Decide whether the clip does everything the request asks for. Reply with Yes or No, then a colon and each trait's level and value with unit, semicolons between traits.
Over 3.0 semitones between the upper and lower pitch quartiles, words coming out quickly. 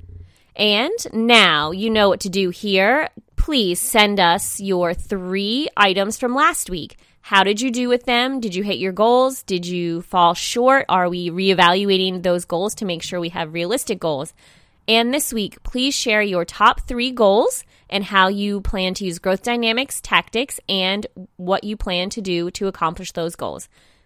No: average, 4.2 semitones; average, 180 wpm